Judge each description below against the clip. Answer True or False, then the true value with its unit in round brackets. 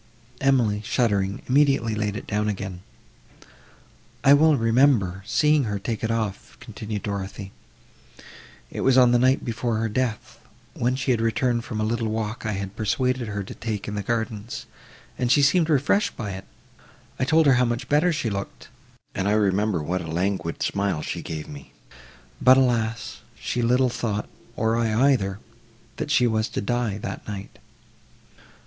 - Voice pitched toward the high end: False (115 Hz)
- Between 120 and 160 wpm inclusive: False (170 wpm)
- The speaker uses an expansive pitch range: False (3.7 semitones)